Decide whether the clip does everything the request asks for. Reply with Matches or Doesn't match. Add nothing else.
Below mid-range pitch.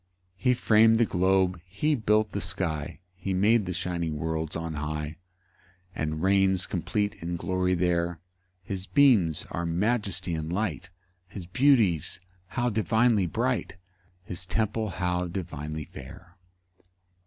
Matches